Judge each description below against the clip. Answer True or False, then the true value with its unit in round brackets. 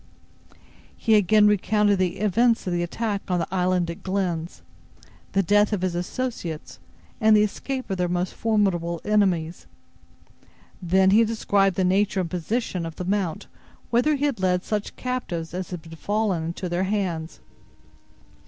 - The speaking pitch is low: False (190 Hz)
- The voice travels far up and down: False (3.2 semitones)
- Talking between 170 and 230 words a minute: False (155 wpm)